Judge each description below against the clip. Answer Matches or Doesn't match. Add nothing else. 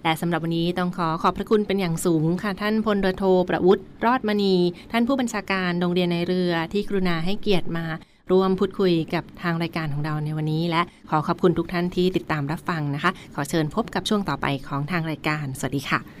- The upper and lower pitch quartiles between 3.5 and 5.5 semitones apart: Doesn't match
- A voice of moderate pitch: Matches